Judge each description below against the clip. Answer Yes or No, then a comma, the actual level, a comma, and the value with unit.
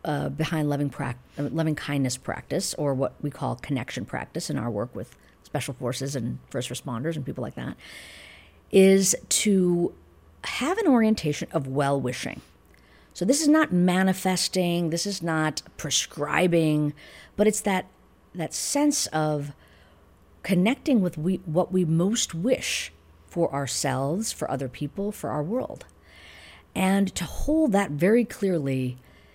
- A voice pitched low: No, medium, 155 Hz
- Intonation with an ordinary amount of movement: No, wide, 5.9 semitones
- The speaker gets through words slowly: No, average, 145 wpm